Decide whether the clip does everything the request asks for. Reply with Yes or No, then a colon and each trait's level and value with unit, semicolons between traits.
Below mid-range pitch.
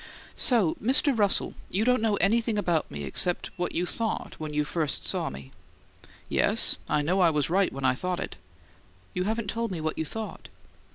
No: medium, 180 Hz